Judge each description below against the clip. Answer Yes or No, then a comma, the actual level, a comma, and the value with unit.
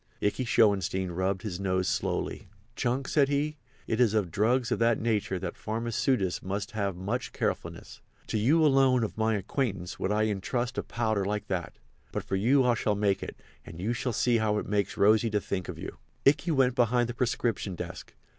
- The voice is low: Yes, low, 110 Hz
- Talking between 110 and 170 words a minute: No, average, 195 wpm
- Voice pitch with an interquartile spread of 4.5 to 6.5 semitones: No, average, 3.8 semitones